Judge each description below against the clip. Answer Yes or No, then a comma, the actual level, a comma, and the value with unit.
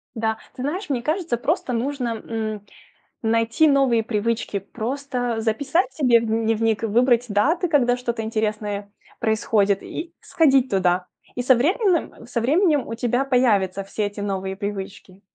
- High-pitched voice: Yes, high, 230 Hz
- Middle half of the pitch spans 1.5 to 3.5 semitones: No, average, 4.0 semitones